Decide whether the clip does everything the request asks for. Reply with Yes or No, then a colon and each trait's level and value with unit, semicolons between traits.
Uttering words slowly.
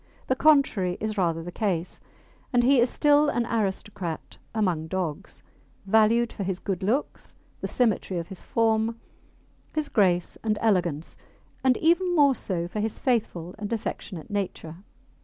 No: average, 150 wpm